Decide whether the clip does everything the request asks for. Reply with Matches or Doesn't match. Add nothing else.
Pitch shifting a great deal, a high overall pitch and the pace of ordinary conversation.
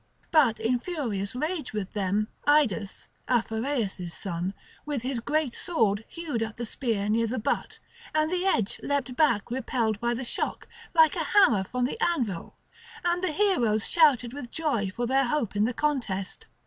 Matches